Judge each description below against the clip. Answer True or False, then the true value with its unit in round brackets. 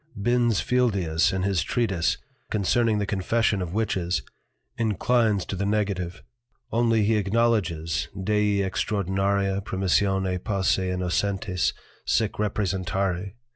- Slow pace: True (105 wpm)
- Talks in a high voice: False (100 Hz)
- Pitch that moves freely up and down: False (2.6 semitones)